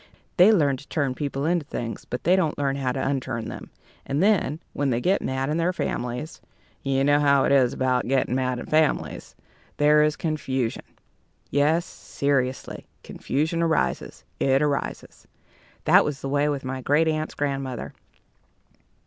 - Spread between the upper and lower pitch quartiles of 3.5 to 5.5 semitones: No, narrow, 2.6 semitones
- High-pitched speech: No, medium, 140 Hz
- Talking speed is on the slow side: No, average, 165 wpm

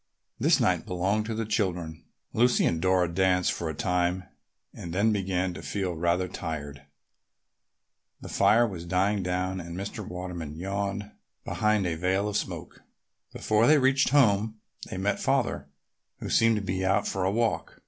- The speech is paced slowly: No, average, 165 wpm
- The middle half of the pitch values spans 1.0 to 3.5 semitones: Yes, average, 2.9 semitones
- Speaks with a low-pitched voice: Yes, very low, 95 Hz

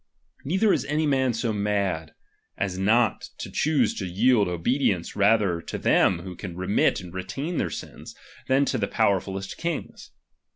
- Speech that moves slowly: No, average, 160 wpm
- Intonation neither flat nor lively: No, wide, 6.0 semitones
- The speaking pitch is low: Yes, low, 100 Hz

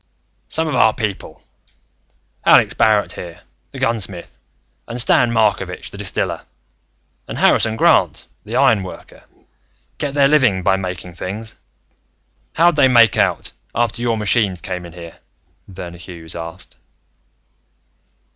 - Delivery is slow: Yes, slow, 125 wpm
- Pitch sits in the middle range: No, low, 105 Hz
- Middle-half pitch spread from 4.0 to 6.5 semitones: Yes, average, 4.6 semitones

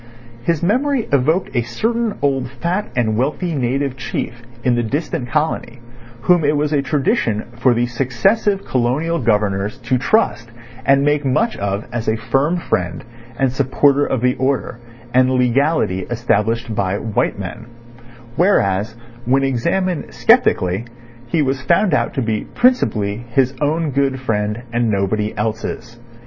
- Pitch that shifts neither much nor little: Yes, average, 4.8 semitones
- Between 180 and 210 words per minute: No, average, 145 wpm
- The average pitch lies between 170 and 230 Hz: No, low, 130 Hz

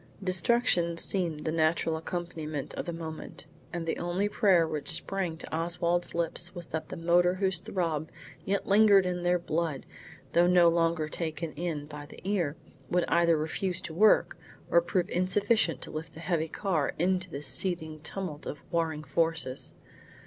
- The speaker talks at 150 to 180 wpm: Yes, average, 165 wpm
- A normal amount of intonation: No, narrow, 2.1 semitones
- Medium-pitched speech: Yes, medium, 170 Hz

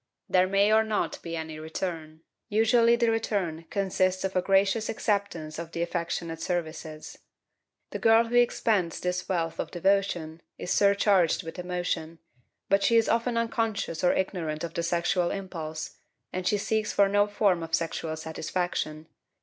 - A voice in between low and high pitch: Yes, medium, 180 Hz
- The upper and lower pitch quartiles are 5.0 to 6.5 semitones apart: No, average, 3.7 semitones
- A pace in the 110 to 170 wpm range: Yes, average, 160 wpm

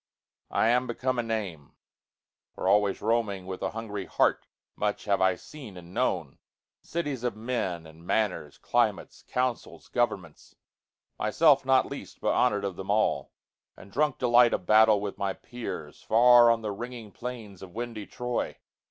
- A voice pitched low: Yes, low, 110 Hz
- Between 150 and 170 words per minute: No, average, 140 wpm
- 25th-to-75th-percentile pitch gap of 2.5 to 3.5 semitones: No, average, 4.1 semitones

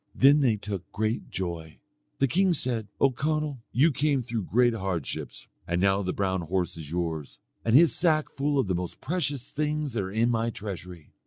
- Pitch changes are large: Yes, wide, 7.2 semitones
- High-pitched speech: No, low, 115 Hz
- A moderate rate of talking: Yes, average, 190 wpm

